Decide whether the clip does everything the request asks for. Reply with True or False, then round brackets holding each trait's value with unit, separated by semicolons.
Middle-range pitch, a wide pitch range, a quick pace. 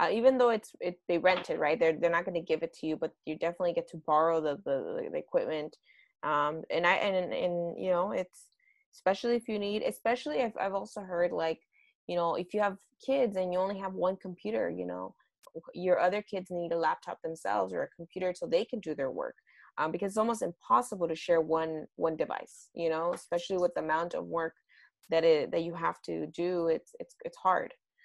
True (180 Hz; 5.9 semitones; 225 wpm)